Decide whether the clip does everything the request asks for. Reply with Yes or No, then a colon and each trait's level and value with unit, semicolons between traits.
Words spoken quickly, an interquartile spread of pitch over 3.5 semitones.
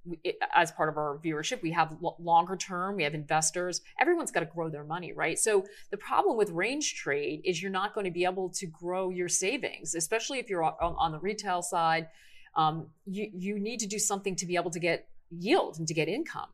Yes: fast, 220 wpm; average, 3.9 semitones